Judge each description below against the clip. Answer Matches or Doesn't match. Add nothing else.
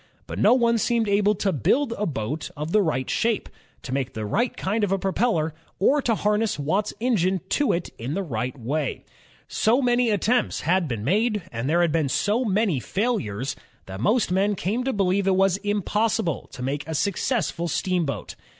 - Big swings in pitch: Matches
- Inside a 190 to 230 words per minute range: Matches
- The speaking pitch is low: Doesn't match